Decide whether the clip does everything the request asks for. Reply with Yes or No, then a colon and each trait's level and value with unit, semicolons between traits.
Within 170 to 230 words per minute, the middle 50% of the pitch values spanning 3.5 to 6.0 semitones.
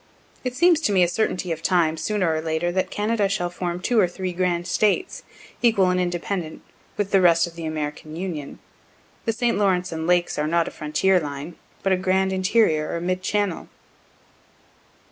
No: average, 190 wpm; average, 2.9 semitones